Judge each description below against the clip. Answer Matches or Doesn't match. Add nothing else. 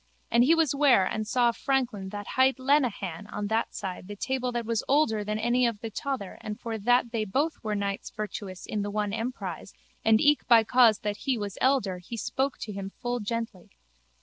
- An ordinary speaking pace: Doesn't match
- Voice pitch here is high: Matches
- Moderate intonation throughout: Matches